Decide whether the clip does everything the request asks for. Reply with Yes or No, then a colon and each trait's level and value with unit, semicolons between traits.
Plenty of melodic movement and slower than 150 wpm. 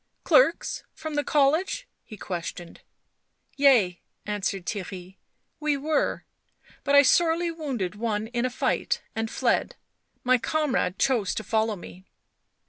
Yes: wide, 6.5 semitones; average, 140 wpm